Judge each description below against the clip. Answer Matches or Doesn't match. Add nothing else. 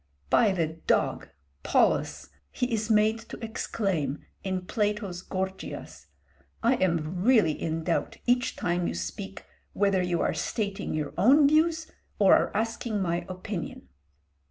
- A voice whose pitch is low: Doesn't match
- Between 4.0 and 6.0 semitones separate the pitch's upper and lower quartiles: Matches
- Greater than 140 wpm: Doesn't match